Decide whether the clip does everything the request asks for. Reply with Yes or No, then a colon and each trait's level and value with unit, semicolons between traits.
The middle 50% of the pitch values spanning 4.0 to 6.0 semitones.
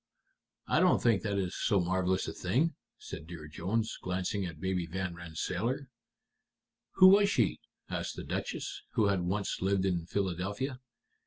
No: average, 3.5 semitones